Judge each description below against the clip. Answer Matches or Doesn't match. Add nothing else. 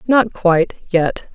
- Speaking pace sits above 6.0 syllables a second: Doesn't match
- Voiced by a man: Doesn't match